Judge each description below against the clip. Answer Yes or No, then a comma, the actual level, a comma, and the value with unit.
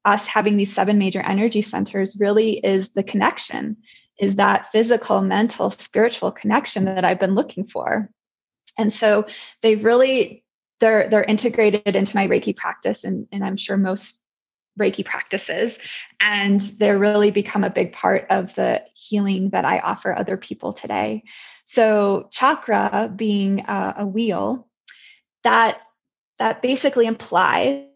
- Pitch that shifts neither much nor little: No, narrow, 2.2 semitones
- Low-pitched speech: No, high, 210 Hz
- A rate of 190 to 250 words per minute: No, average, 140 wpm